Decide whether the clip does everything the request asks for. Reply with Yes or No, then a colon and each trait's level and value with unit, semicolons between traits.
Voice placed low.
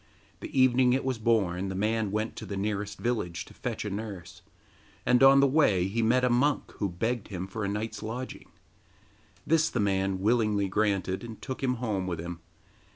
Yes: low, 110 Hz